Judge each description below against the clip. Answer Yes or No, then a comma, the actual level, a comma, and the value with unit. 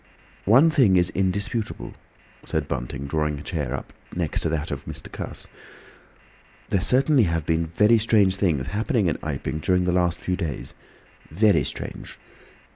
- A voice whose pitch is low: Yes, very low, 90 Hz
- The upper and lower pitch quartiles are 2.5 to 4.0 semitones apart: No, average, 5.2 semitones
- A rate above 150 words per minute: No, average, 145 wpm